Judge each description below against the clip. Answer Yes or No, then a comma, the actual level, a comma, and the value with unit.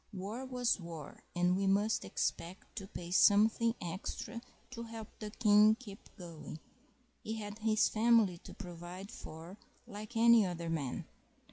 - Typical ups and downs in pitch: Yes, average, 4.1 semitones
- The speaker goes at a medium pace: Yes, average, 145 wpm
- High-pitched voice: Yes, high, 205 Hz